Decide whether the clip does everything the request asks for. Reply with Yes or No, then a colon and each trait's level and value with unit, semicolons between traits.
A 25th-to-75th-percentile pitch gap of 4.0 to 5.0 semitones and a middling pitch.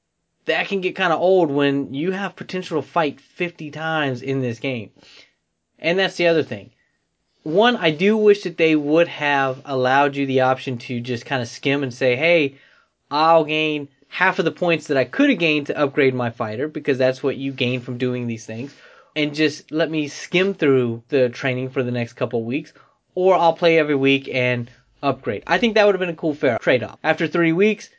Yes: average, 4.6 semitones; medium, 145 Hz